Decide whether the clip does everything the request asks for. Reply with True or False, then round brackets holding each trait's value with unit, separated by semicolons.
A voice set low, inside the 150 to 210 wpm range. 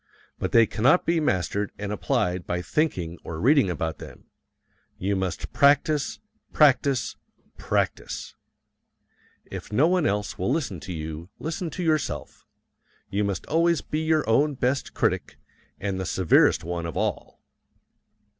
False (110 Hz; 140 wpm)